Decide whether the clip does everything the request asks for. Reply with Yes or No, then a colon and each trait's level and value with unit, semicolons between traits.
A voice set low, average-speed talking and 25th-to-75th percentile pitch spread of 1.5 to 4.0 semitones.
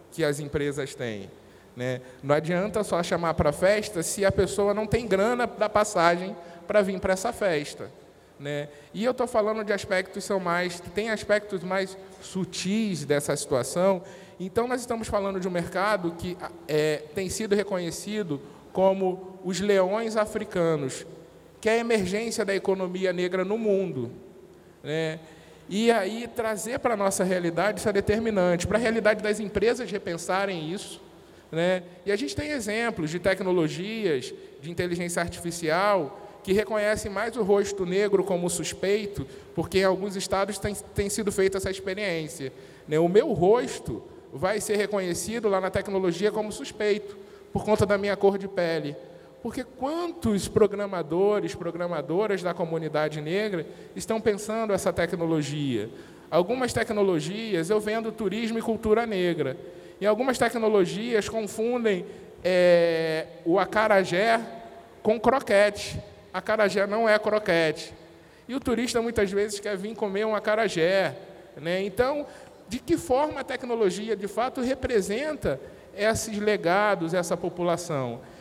No: high, 195 Hz; average, 145 wpm; average, 3.4 semitones